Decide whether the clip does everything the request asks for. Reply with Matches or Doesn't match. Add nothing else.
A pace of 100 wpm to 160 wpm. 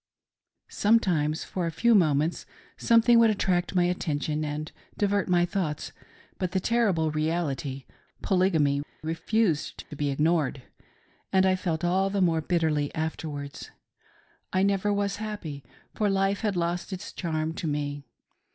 Matches